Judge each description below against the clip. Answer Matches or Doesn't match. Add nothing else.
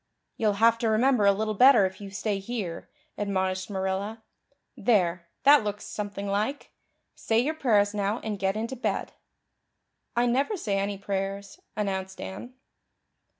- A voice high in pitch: Matches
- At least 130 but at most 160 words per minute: Matches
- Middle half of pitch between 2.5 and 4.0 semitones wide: Matches